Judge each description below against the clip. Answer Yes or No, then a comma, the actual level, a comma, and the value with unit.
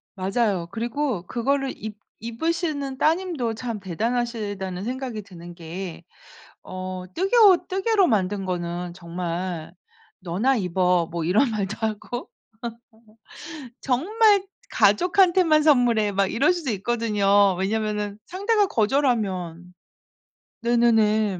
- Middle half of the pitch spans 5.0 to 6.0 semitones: No, wide, 6.5 semitones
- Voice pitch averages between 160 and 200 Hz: No, high, 220 Hz